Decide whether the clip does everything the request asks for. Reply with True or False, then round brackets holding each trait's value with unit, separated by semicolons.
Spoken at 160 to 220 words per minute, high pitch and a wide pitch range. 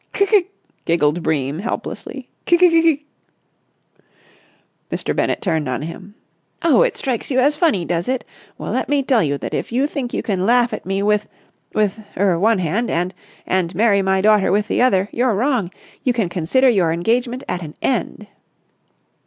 True (165 wpm; 210 Hz; 6.3 semitones)